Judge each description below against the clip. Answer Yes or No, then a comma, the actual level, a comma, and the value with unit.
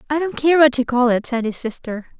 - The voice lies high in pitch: Yes, very high, 260 Hz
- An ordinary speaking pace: No, fast, 275 wpm